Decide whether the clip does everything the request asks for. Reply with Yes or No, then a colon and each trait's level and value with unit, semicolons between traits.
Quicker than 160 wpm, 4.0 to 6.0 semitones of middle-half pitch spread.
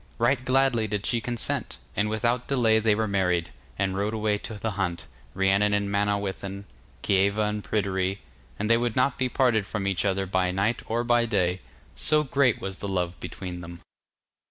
No: average, 180 wpm; average, 3.1 semitones